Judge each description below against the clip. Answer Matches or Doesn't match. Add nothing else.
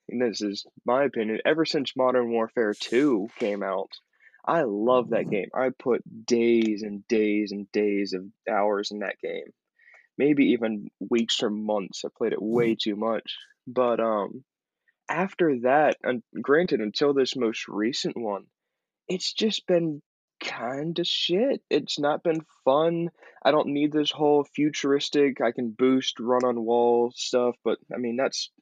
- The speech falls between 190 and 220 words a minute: Doesn't match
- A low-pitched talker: Matches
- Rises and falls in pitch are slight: Doesn't match